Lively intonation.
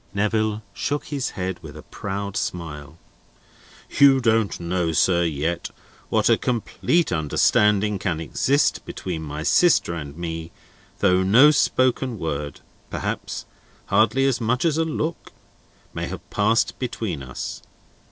Yes: wide, 7.0 semitones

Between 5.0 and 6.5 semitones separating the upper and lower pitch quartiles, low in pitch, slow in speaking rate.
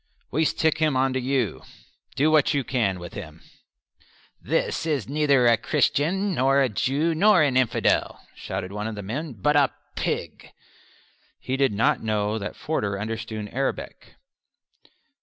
No: wide, 5.5 semitones; low, 130 Hz; average, 155 wpm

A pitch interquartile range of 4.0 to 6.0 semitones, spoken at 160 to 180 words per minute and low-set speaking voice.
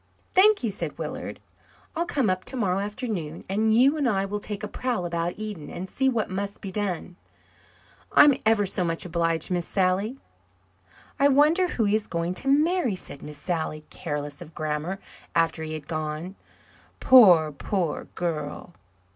No: average, 5.2 semitones; average, 165 wpm; high, 190 Hz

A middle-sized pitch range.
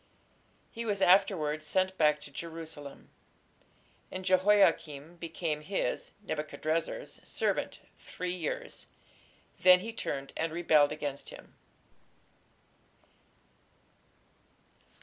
Yes: average, 3.7 semitones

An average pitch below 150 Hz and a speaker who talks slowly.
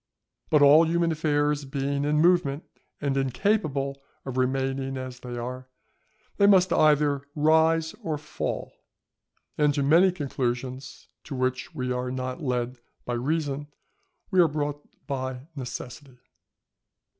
Yes: medium, 140 Hz; slow, 130 wpm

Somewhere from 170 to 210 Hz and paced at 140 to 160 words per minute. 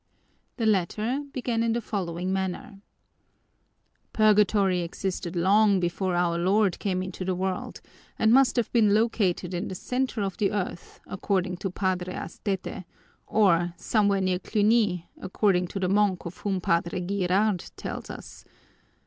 Yes: high, 190 Hz; average, 145 wpm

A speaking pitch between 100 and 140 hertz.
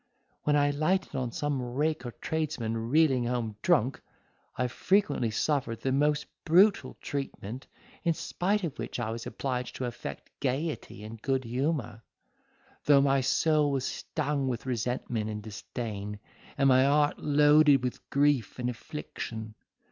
Yes: low, 135 Hz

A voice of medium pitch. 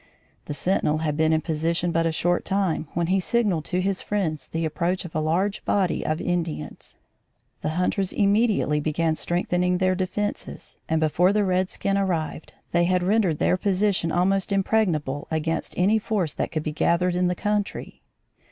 Yes: medium, 180 Hz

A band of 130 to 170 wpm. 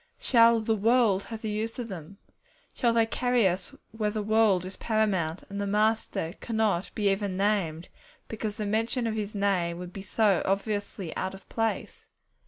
No: average, 180 wpm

